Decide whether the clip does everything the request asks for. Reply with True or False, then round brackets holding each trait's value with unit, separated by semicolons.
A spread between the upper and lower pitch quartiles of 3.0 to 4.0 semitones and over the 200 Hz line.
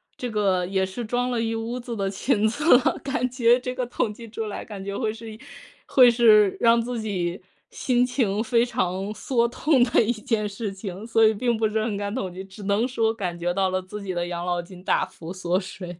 True (3.7 semitones; 215 Hz)